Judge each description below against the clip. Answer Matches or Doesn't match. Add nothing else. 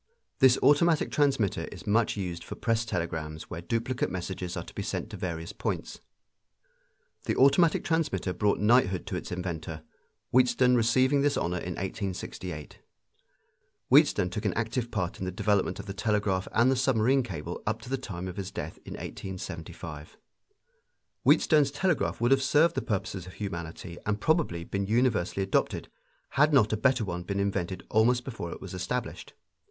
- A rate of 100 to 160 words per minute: Doesn't match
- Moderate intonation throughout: Doesn't match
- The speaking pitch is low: Matches